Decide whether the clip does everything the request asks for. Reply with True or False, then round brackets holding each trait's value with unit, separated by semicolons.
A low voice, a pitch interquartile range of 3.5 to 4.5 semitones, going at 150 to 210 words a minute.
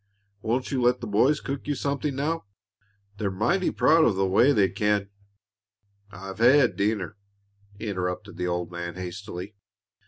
False (105 Hz; 5.3 semitones; 155 wpm)